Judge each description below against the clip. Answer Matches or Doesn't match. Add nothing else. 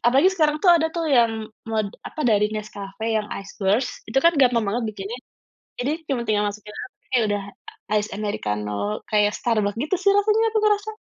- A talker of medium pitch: Doesn't match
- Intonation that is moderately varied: Doesn't match